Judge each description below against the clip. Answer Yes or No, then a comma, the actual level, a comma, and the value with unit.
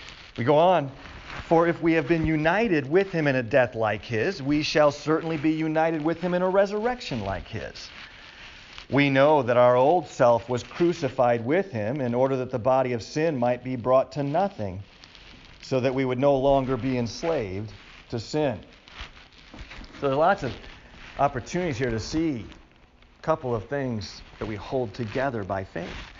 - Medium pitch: No, low, 130 Hz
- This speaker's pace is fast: No, average, 180 wpm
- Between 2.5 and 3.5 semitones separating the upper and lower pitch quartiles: No, average, 5.3 semitones